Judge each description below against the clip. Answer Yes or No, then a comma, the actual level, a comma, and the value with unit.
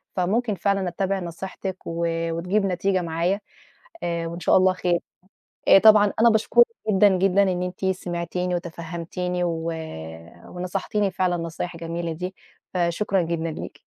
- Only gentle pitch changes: Yes, narrow, 2.3 semitones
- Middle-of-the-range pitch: Yes, medium, 180 Hz